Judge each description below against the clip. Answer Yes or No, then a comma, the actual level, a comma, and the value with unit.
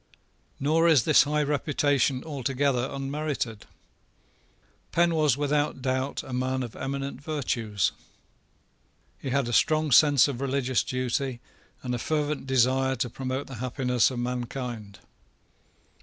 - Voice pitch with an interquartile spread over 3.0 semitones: No, narrow, 2.5 semitones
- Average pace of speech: No, slow, 125 wpm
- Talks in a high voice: No, low, 135 Hz